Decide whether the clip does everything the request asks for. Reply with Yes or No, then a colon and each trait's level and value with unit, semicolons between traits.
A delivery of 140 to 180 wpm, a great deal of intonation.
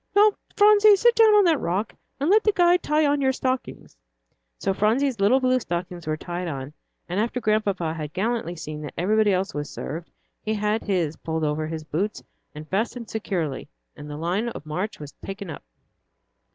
No: average, 190 wpm; wide, 8.0 semitones